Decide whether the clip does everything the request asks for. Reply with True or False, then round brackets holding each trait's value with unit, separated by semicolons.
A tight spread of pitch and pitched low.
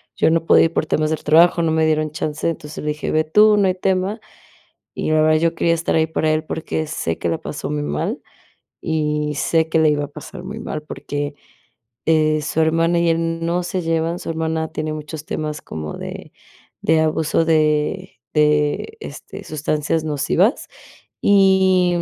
False (1.7 semitones; 160 Hz)